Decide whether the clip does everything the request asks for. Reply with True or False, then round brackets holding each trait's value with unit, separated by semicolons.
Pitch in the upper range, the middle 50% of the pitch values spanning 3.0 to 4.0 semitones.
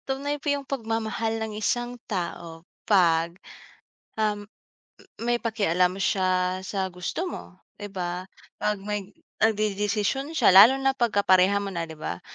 True (205 Hz; 3.6 semitones)